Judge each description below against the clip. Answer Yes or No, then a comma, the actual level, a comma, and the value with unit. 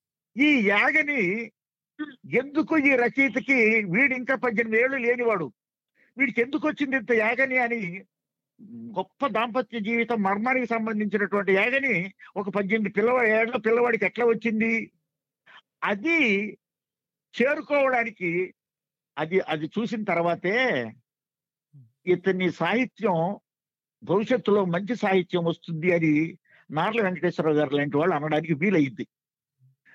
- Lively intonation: Yes, wide, 6.0 semitones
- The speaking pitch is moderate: No, high, 210 Hz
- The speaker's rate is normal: Yes, average, 90 wpm